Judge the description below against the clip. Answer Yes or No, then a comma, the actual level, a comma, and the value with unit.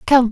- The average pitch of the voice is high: Yes, high, 245 Hz